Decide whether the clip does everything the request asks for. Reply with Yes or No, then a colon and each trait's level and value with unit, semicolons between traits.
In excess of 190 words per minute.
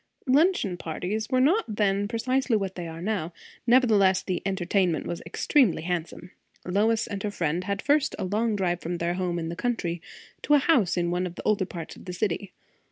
Yes: average, 200 wpm